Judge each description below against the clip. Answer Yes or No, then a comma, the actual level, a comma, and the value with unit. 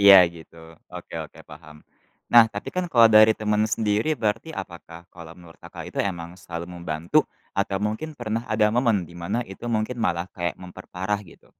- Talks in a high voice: No, low, 100 Hz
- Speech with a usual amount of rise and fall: Yes, average, 4.1 semitones